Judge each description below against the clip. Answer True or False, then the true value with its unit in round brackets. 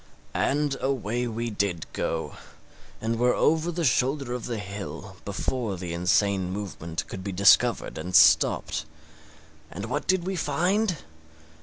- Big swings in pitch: True (6.4 semitones)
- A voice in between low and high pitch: False (115 Hz)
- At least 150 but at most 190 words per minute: False (140 wpm)